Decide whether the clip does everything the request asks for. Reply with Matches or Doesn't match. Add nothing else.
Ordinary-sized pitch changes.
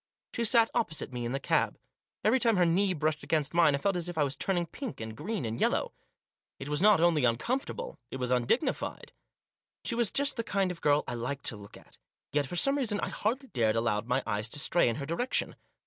Doesn't match